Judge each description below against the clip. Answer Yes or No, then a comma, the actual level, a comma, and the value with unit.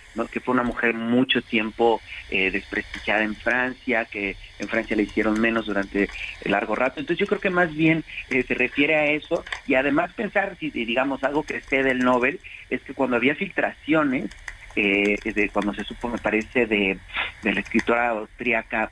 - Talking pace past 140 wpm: Yes, average, 185 wpm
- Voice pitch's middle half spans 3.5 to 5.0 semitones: Yes, average, 3.9 semitones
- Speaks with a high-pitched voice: No, low, 120 Hz